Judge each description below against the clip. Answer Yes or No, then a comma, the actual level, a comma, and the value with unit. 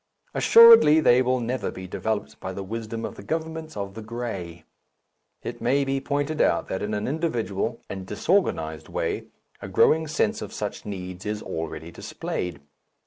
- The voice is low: Yes, low, 115 Hz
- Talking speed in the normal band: Yes, average, 165 wpm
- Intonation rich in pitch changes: Yes, wide, 7.0 semitones